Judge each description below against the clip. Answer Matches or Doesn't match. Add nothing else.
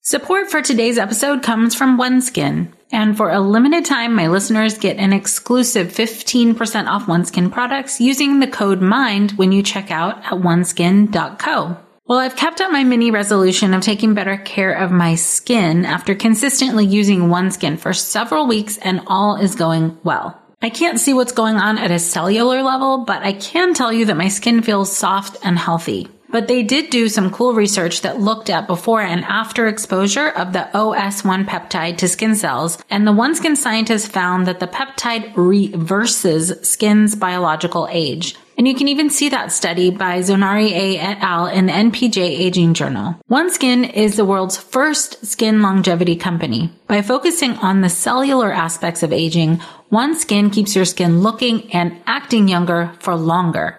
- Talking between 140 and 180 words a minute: Matches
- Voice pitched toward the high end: Matches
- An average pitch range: Matches